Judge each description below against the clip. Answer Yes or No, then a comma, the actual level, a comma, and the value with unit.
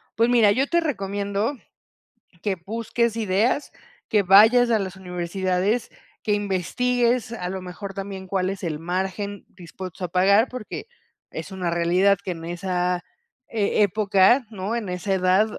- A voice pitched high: Yes, high, 195 Hz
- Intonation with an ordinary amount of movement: Yes, average, 3.2 semitones